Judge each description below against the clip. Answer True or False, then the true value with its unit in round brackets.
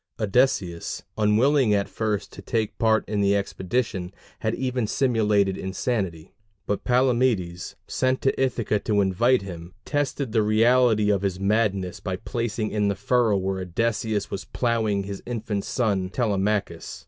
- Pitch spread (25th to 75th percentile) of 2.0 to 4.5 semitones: True (3.4 semitones)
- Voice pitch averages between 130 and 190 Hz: False (105 Hz)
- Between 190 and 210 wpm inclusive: False (145 wpm)